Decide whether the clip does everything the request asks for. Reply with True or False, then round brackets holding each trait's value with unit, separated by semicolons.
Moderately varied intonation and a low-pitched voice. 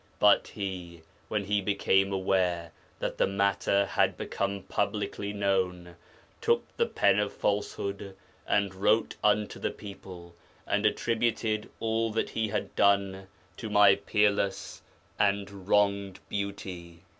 False (1.4 semitones; 100 Hz)